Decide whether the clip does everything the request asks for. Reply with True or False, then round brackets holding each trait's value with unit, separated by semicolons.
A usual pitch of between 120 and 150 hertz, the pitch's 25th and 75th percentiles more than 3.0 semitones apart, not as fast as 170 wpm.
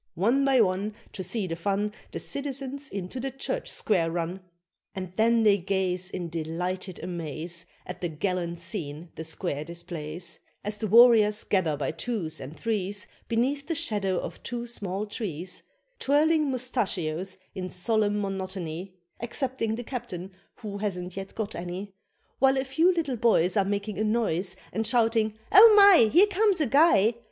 False (205 Hz; 4.9 semitones; 160 wpm)